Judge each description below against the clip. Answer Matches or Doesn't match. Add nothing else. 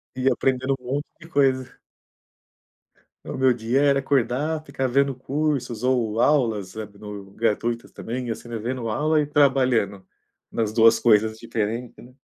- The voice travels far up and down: Doesn't match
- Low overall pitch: Matches